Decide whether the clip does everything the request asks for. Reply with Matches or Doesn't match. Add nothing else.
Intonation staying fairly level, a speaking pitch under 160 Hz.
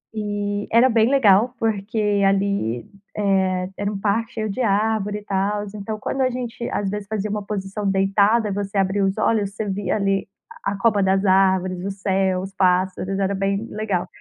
Doesn't match